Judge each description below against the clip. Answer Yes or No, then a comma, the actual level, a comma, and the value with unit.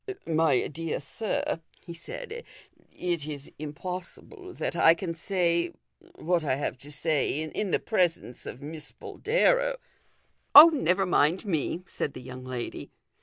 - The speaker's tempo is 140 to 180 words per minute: Yes, average, 155 wpm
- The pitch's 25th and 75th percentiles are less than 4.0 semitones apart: No, average, 4.3 semitones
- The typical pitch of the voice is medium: Yes, medium, 165 Hz